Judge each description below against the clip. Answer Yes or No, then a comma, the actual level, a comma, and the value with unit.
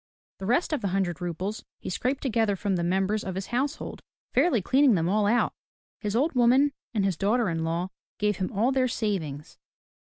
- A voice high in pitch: Yes, high, 205 Hz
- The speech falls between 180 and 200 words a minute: Yes, average, 195 wpm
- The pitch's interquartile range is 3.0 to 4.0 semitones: No, average, 4.8 semitones